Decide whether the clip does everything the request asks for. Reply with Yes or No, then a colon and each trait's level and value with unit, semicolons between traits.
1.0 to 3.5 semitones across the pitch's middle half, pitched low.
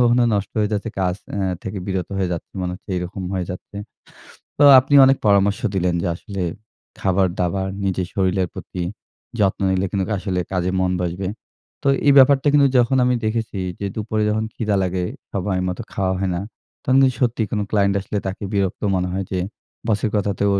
Yes: average, 2.7 semitones; low, 100 Hz